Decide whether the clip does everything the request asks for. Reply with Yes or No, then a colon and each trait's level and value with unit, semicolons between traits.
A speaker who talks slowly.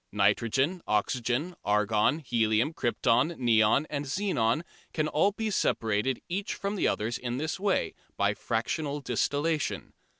Yes: slow, 130 wpm